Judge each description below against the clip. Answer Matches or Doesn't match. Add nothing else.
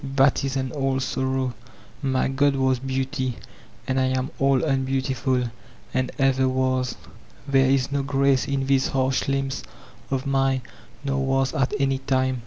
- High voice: Doesn't match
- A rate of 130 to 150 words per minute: Doesn't match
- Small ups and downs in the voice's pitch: Matches